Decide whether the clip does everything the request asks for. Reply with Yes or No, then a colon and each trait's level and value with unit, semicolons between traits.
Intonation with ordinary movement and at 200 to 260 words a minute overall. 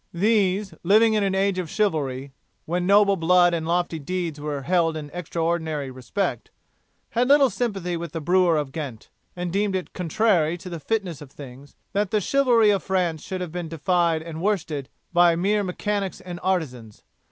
No: average, 3.8 semitones; average, 175 wpm